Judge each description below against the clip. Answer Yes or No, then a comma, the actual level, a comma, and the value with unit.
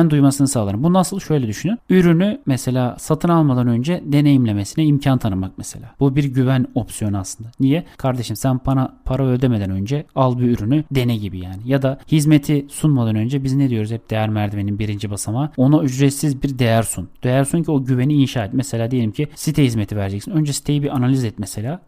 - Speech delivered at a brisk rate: Yes, fast, 195 wpm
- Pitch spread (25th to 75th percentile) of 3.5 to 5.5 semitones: Yes, average, 4.3 semitones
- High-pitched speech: No, low, 130 Hz